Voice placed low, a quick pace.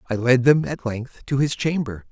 Yes: low, 125 Hz; fast, 225 wpm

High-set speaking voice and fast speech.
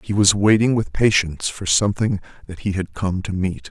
No: very low, 95 Hz; fast, 210 wpm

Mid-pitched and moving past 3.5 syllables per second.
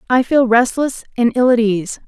No: high, 240 Hz; 4.8 syllables/s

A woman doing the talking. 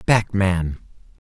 No: male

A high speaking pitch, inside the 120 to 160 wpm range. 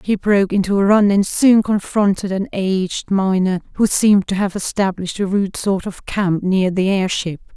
No: high, 195 Hz; average, 190 wpm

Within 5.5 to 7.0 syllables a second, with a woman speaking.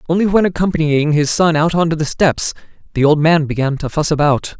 No: 5.8 syllables/s; male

